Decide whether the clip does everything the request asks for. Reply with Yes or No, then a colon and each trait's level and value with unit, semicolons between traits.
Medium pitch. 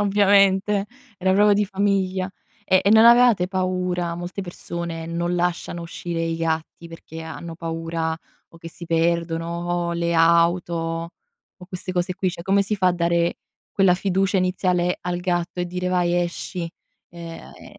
Yes: medium, 175 Hz